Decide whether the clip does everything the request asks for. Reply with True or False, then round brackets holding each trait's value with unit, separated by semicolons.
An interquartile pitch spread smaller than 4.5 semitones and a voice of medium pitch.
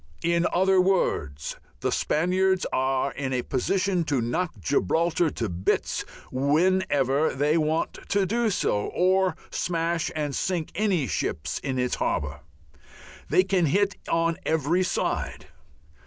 False (5.6 semitones; 165 Hz)